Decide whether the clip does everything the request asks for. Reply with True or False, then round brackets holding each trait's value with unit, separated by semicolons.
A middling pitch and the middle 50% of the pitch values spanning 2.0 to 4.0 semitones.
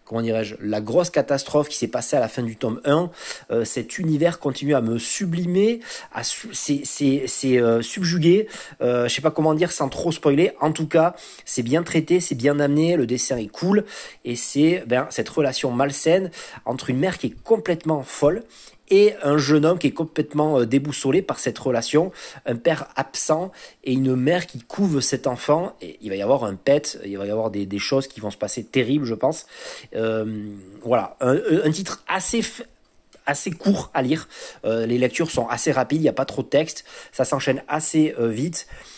False (145 Hz; 5.2 semitones)